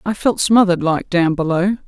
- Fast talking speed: No, average, 190 wpm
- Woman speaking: Yes, female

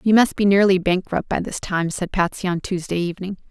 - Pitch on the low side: No, medium, 185 Hz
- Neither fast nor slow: No, fast, 225 wpm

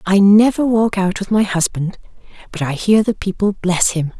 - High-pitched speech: Yes, high, 195 Hz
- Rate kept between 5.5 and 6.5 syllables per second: No, 4.8 syllables/s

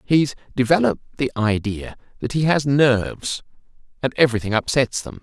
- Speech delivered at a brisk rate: No, average, 140 wpm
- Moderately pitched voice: No, low, 125 Hz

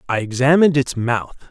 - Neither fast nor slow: Yes, average, 160 wpm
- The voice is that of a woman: No, male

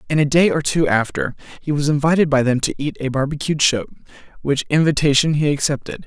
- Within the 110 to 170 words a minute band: No, average, 200 wpm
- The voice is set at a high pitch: No, medium, 145 Hz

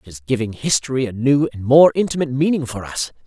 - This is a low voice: Yes, low, 130 Hz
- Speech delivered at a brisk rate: Yes, fast, 220 wpm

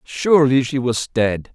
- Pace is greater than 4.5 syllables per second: No, 4.1 syllables/s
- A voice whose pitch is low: Yes, low, 130 Hz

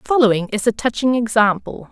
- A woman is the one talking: Yes, female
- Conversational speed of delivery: Yes, average, 155 wpm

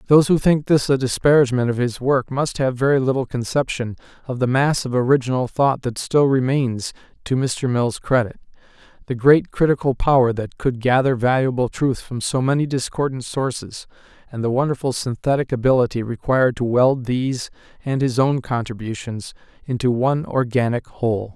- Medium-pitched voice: No, low, 130 Hz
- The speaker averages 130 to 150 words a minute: No, average, 165 wpm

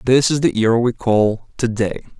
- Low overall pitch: Yes, low, 115 Hz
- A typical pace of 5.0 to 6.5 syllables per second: No, 4.7 syllables/s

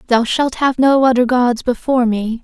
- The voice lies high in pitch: Yes, high, 245 Hz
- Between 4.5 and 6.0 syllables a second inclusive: Yes, 4.9 syllables/s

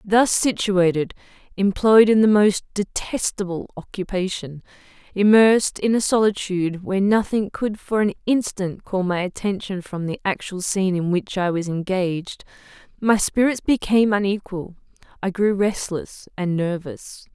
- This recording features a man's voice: No, female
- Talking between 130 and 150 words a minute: Yes, slow, 135 wpm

